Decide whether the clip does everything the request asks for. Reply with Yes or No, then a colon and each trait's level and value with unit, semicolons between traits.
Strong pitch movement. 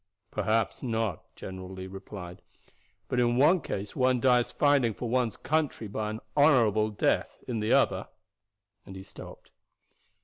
No: average, 4.0 semitones